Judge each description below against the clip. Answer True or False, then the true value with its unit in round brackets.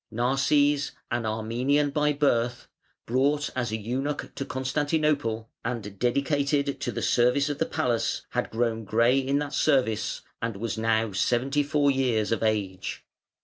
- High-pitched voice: False (125 Hz)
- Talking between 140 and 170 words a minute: True (145 wpm)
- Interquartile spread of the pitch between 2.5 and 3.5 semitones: False (4.0 semitones)